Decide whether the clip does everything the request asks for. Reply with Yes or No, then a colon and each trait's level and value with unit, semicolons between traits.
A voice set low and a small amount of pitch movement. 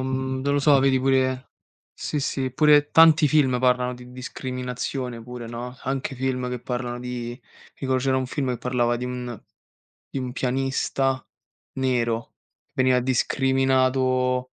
Yes: low, 130 Hz; narrow, 1.2 semitones